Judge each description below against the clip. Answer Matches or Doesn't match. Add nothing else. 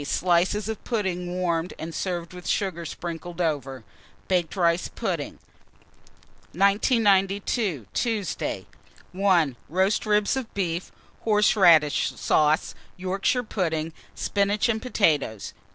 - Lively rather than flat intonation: Doesn't match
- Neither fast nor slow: Doesn't match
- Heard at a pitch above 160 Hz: Matches